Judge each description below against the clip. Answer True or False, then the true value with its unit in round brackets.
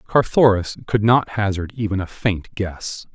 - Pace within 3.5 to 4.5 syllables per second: True (4.3 syllables/s)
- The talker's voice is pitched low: True (100 Hz)